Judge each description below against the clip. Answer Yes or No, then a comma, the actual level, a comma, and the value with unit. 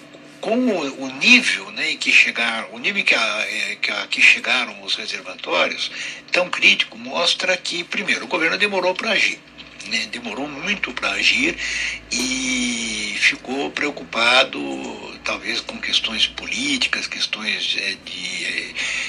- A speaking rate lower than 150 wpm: Yes, average, 130 wpm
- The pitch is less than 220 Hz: No, high, 225 Hz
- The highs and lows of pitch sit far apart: Yes, wide, 6.8 semitones